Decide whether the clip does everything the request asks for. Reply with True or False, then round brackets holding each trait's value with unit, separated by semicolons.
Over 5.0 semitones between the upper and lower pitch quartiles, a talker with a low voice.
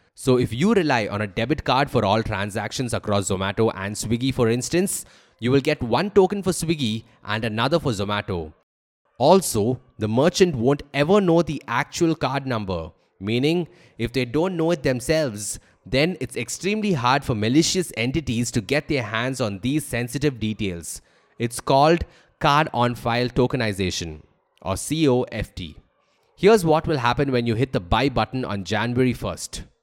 True (5.5 semitones; 125 Hz)